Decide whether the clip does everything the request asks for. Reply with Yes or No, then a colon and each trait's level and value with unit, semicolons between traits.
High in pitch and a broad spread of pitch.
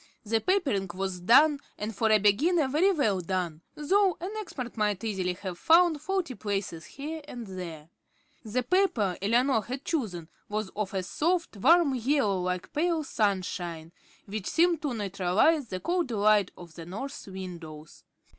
Yes: high, 215 Hz; wide, 8.2 semitones